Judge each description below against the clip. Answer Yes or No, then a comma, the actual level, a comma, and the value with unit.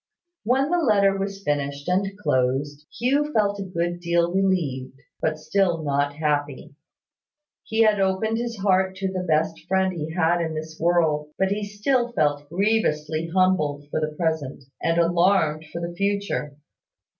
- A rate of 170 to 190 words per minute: No, average, 155 wpm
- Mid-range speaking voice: Yes, medium, 175 Hz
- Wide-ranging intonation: No, average, 4.4 semitones